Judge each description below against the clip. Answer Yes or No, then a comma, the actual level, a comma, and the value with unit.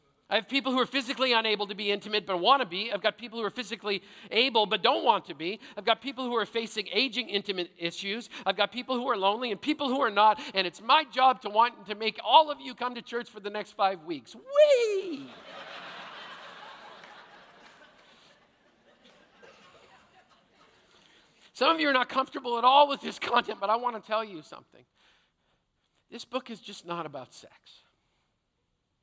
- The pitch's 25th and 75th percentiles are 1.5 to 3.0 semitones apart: No, average, 4.1 semitones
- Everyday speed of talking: Yes, average, 190 wpm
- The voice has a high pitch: Yes, high, 230 Hz